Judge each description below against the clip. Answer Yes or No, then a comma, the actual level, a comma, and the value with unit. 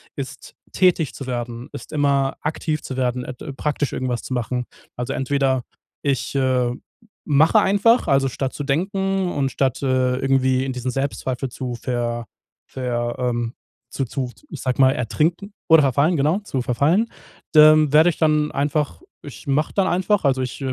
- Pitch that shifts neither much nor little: Yes, average, 3.3 semitones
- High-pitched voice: No, low, 135 Hz